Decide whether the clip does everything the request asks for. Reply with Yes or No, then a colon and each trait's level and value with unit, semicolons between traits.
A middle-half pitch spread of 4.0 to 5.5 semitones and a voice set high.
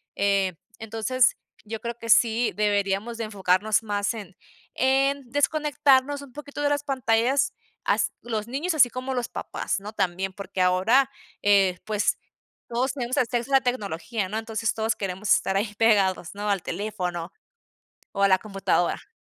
Yes: average, 4.3 semitones; high, 220 Hz